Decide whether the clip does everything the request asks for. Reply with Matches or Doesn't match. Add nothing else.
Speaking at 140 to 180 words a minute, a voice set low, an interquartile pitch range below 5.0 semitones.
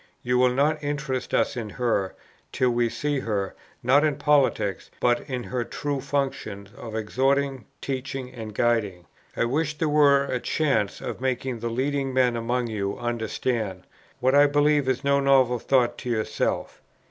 Matches